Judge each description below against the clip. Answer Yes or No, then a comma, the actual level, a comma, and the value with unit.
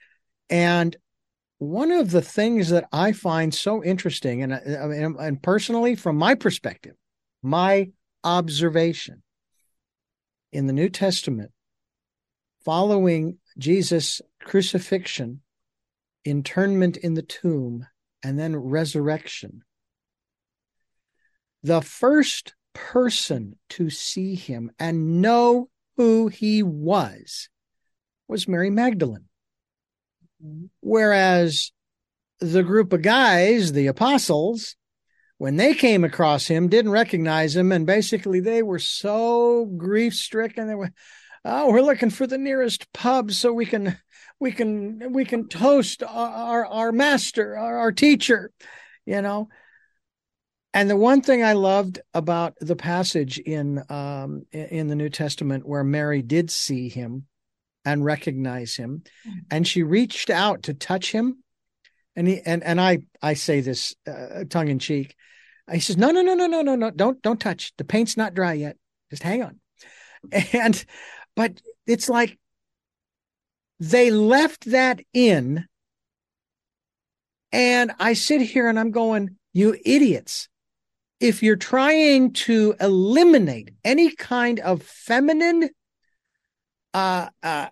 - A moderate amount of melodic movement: No, wide, 6.6 semitones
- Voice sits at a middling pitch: No, high, 195 Hz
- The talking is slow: Yes, slow, 125 wpm